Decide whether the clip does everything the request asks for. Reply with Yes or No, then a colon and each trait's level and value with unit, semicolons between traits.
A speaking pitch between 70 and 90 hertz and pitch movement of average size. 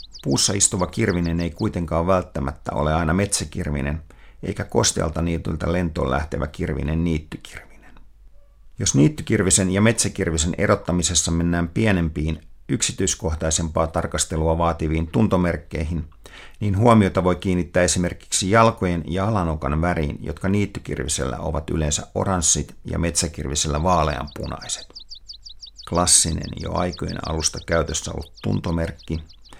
Yes: very low, 85 Hz; average, 3.0 semitones